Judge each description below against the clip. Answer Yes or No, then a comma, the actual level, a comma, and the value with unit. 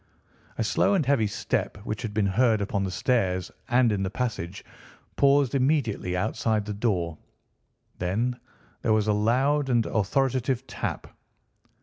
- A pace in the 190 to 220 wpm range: No, average, 145 wpm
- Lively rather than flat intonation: No, average, 4.2 semitones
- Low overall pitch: Yes, low, 110 Hz